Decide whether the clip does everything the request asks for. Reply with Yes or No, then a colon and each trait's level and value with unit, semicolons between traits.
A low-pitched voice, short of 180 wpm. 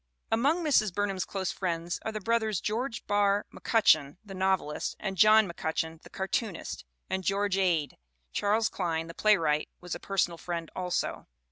No: high, 195 Hz; average, 155 wpm